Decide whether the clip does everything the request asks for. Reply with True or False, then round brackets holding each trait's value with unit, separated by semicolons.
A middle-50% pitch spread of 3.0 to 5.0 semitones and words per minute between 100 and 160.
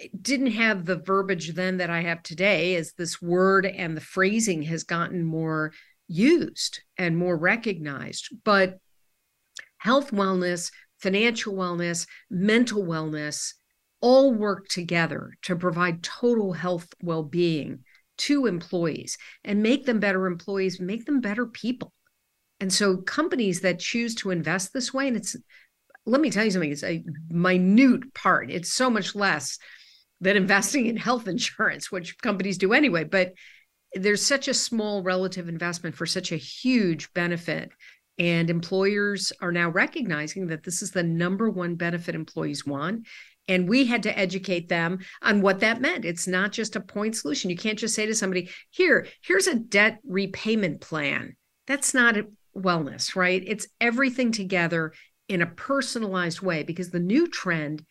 True (4.2 semitones; 155 wpm)